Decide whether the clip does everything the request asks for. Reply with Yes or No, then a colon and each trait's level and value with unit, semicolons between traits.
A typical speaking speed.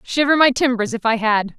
No: fast, 230 wpm